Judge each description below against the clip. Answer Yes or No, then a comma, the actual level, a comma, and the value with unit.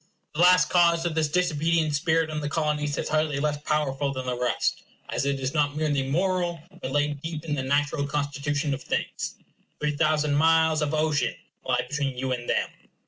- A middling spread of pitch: No, narrow, 2.1 semitones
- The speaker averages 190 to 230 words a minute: Yes, average, 195 wpm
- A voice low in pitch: No, medium, 150 Hz